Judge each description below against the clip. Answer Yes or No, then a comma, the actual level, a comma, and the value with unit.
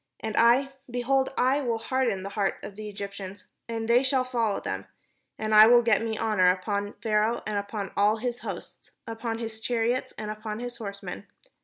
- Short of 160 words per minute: No, average, 185 wpm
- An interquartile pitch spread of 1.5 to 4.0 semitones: Yes, average, 2.7 semitones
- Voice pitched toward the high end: Yes, high, 225 Hz